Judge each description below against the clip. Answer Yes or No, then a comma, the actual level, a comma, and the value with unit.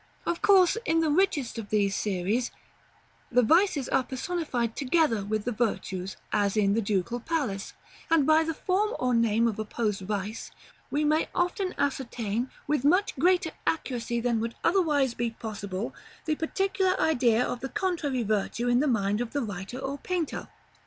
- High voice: Yes, high, 245 Hz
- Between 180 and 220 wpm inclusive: No, average, 165 wpm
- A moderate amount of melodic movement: No, wide, 6.7 semitones